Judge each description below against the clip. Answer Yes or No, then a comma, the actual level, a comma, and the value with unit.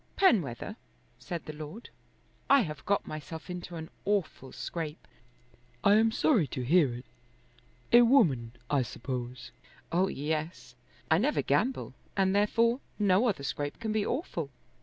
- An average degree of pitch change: No, wide, 6.7 semitones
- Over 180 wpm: No, average, 140 wpm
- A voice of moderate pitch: Yes, medium, 175 Hz